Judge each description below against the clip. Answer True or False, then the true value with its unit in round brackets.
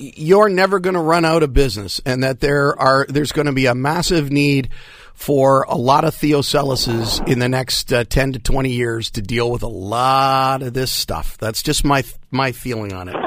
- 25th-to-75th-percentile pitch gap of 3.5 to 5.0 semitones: False (3.0 semitones)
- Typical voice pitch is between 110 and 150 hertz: True (135 Hz)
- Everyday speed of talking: False (215 wpm)